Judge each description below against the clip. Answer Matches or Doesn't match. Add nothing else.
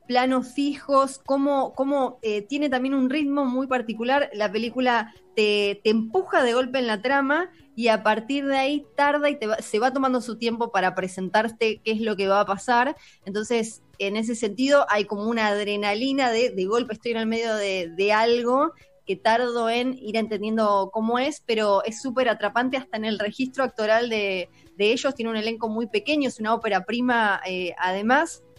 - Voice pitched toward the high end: Matches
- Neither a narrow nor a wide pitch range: Matches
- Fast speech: Matches